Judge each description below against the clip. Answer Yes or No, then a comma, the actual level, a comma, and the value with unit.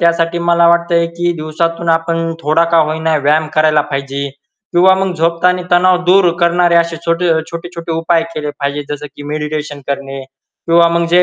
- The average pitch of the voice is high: No, medium, 165 Hz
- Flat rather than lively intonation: Yes, narrow, 1.8 semitones